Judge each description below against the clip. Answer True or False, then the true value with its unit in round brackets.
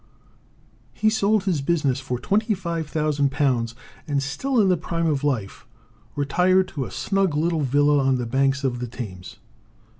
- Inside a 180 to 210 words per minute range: False (150 wpm)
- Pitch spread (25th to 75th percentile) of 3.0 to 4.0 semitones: False (4.8 semitones)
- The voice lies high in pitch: False (145 Hz)